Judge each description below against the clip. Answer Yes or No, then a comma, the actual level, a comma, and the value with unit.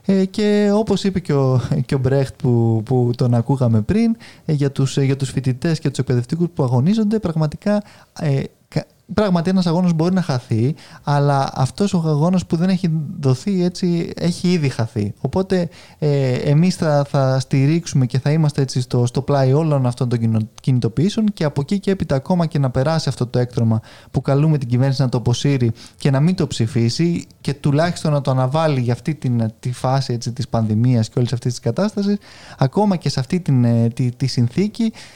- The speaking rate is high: Yes, fast, 180 wpm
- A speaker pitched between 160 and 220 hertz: No, medium, 140 Hz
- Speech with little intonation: No, average, 5.2 semitones